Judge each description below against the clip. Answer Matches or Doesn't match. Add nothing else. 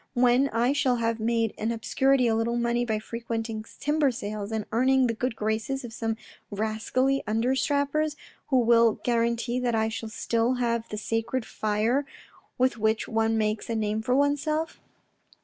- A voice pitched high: Matches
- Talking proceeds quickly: Doesn't match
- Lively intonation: Doesn't match